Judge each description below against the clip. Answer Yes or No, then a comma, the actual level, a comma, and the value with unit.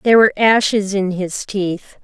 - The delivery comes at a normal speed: Yes, average, 175 wpm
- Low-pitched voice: No, high, 200 Hz